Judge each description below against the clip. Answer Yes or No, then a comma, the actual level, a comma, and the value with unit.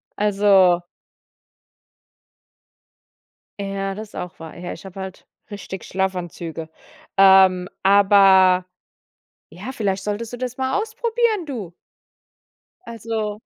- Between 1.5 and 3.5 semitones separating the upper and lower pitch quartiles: Yes, average, 2.9 semitones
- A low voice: No, high, 195 Hz